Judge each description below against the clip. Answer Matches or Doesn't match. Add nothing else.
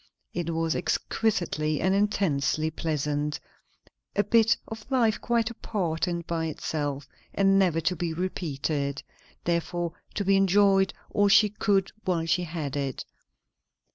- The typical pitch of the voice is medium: Matches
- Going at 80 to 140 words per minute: Matches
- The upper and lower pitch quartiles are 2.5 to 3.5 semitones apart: Doesn't match